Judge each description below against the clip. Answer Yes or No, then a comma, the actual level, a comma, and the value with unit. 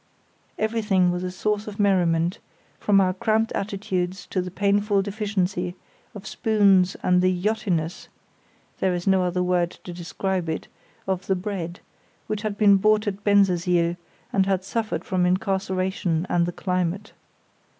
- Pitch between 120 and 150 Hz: No, high, 190 Hz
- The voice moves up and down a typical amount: No, narrow, 2.3 semitones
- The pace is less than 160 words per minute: Yes, average, 150 wpm